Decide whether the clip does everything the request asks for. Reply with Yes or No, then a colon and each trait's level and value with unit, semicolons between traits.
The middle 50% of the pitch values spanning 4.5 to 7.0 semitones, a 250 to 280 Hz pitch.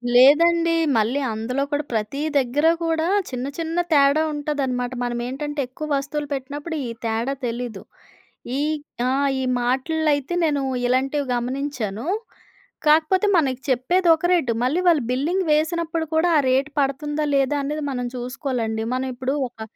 No: average, 3.5 semitones; very high, 275 Hz